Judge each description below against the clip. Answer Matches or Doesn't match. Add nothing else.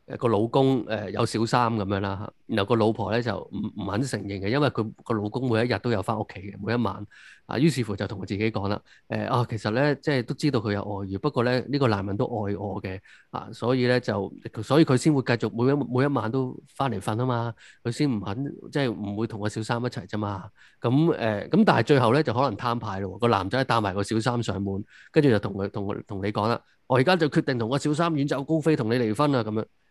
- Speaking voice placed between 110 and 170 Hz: Matches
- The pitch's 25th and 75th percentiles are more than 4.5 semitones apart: Doesn't match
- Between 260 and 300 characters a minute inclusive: Doesn't match